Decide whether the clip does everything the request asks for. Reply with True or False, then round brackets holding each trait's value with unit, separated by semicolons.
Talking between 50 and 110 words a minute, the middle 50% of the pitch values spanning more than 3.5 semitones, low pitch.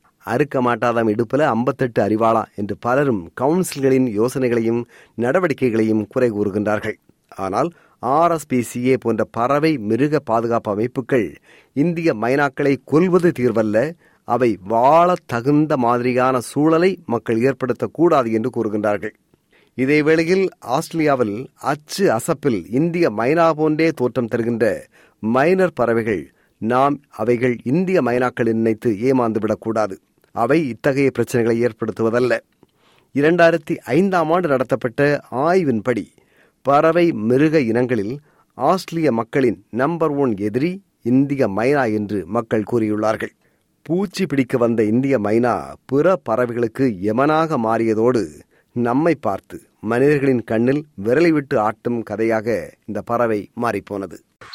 True (100 wpm; 4.7 semitones; 125 Hz)